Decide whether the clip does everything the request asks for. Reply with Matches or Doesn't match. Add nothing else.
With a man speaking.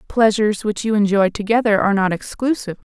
Doesn't match